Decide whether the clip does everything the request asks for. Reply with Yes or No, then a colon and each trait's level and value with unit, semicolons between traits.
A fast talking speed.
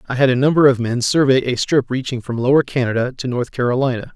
Yes: fast, 230 wpm